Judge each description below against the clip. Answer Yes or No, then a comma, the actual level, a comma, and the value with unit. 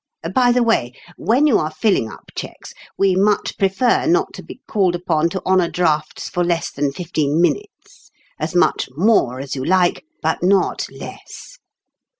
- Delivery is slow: No, average, 165 wpm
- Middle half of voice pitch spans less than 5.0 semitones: No, average, 5.3 semitones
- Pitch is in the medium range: Yes, medium, 180 Hz